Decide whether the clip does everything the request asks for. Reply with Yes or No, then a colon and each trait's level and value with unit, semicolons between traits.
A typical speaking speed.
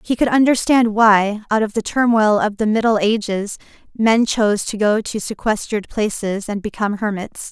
Yes: average, 175 wpm